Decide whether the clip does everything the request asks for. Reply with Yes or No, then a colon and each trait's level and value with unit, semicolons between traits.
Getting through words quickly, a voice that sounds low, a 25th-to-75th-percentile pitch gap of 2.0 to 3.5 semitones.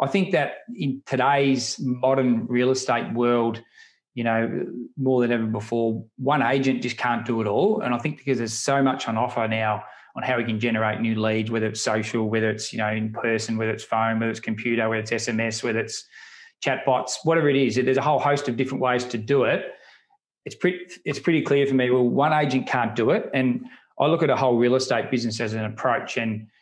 Yes: fast, 225 wpm; low, 120 Hz; average, 3.1 semitones